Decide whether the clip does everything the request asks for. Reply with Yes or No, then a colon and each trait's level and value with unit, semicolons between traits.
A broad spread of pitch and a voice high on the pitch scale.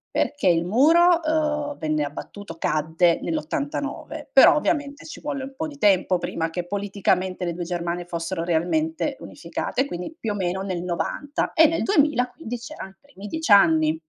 Yes: wide, 9.0 semitones; high, 205 Hz